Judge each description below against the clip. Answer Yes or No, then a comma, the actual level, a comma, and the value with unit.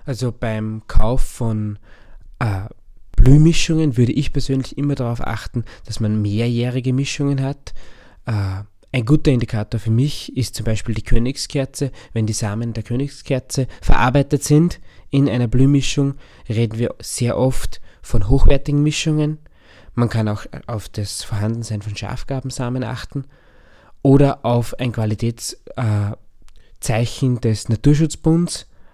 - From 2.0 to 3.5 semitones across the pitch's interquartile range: No, average, 3.9 semitones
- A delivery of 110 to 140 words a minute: Yes, slow, 125 wpm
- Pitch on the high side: No, low, 120 Hz